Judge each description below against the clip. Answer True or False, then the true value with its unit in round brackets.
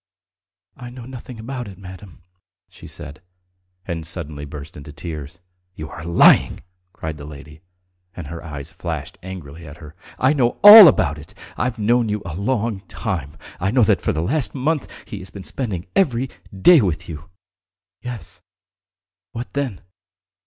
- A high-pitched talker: False (95 Hz)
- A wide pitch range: True (7.7 semitones)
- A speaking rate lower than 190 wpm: True (160 wpm)